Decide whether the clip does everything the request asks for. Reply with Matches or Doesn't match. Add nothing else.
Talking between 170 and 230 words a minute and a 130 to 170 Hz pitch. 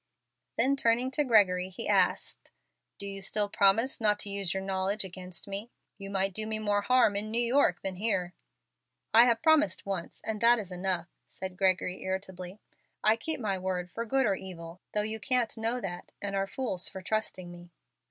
Doesn't match